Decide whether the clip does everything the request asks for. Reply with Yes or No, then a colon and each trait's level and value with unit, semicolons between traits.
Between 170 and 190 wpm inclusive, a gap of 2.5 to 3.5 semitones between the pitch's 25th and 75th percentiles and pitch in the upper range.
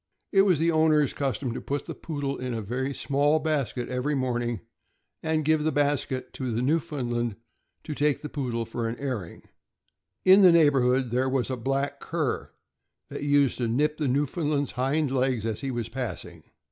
No: average, 180 wpm; average, 3.2 semitones; low, 135 Hz